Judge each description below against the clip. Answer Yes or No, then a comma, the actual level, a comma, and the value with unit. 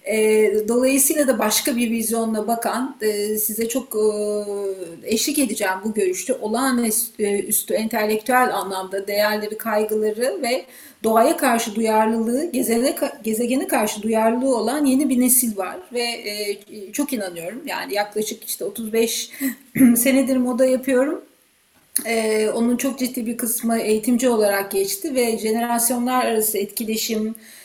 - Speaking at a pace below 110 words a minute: No, average, 115 wpm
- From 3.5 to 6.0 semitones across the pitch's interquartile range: No, average, 2.9 semitones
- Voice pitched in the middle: No, high, 230 Hz